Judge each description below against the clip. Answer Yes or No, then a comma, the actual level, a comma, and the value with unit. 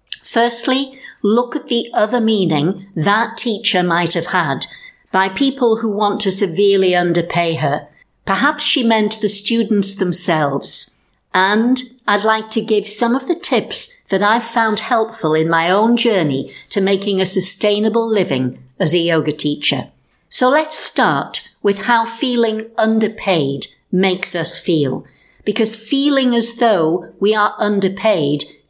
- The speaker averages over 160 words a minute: No, average, 140 wpm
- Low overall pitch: No, high, 205 Hz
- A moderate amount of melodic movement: Yes, average, 4.6 semitones